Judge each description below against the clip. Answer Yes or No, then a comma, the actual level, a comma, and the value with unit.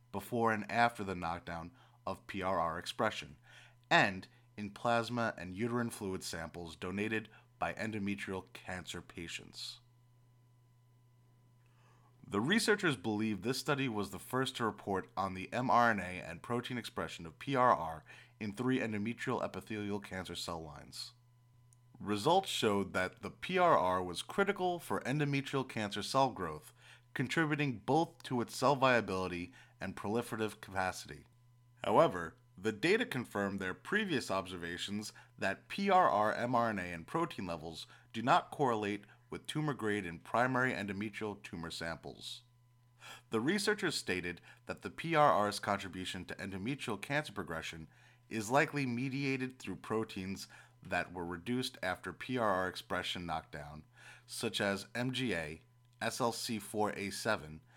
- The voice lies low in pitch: Yes, low, 115 Hz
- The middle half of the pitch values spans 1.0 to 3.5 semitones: No, average, 4.3 semitones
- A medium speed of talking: No, slow, 120 wpm